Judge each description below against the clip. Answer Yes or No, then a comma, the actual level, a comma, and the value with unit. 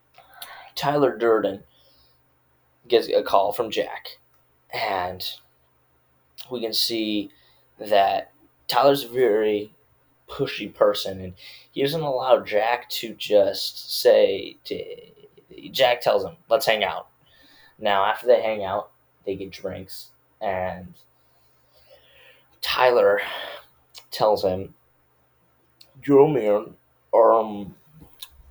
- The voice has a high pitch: No, low, 115 Hz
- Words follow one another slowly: Yes, slow, 100 wpm